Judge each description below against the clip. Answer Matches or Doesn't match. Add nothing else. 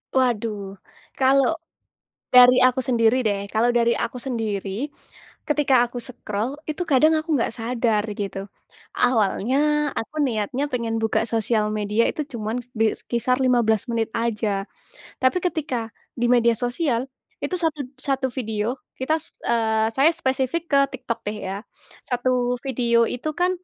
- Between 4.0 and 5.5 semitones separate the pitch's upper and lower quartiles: Doesn't match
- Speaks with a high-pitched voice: Matches